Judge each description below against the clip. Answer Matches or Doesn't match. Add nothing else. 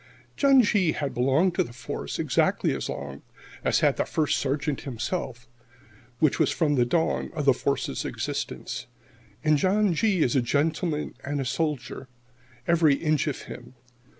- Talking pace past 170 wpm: Doesn't match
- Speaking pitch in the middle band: Matches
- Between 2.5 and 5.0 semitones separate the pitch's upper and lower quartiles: Matches